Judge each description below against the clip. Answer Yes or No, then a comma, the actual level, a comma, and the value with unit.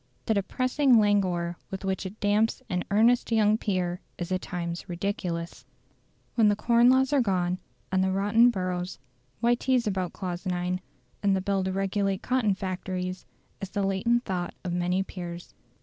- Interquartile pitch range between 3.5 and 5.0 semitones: No, average, 3.0 semitones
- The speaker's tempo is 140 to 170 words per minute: Yes, average, 165 wpm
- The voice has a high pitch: Yes, high, 195 Hz